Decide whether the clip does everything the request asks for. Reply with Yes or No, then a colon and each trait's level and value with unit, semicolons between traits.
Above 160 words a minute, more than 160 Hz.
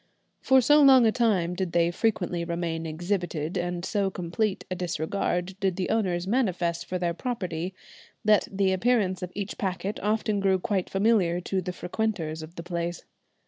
Yes: average, 170 wpm; medium, 185 Hz